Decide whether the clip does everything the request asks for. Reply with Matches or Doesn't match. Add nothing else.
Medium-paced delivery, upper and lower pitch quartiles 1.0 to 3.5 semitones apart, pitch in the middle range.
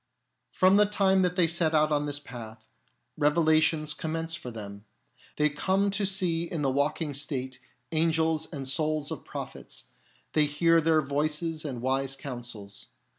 Matches